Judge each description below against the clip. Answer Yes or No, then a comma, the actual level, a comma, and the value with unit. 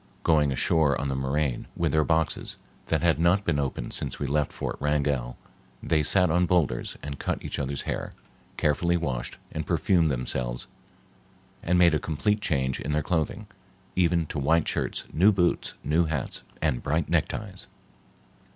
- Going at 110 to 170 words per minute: Yes, average, 165 wpm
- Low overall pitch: Yes, very low, 75 Hz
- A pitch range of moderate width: Yes, average, 3.4 semitones